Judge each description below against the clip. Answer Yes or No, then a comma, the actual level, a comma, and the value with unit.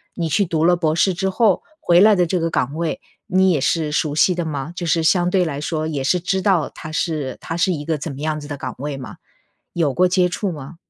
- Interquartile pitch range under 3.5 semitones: Yes, average, 3.1 semitones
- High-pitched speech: No, medium, 165 Hz